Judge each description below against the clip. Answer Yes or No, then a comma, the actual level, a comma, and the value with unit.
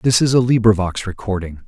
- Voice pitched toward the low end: Yes, low, 105 Hz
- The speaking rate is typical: Yes, average, 180 wpm